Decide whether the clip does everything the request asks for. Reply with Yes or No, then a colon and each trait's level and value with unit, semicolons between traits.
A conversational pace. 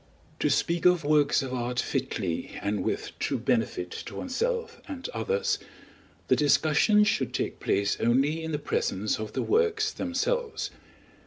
Yes: average, 150 wpm